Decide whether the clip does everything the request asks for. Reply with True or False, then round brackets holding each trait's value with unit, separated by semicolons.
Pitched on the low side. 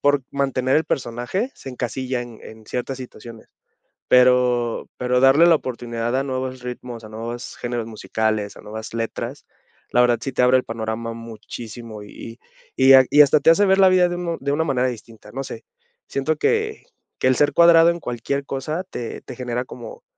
True (125 Hz)